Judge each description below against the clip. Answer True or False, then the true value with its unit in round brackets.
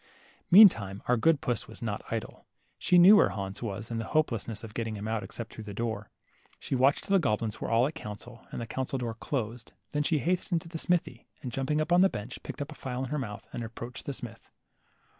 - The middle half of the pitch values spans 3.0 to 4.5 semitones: False (5.2 semitones)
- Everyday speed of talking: False (240 wpm)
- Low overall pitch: True (120 Hz)